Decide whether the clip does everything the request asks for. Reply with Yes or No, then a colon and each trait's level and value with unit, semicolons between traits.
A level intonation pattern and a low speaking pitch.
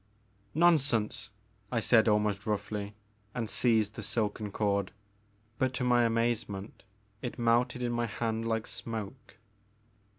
Yes: narrow, 2.3 semitones; low, 115 Hz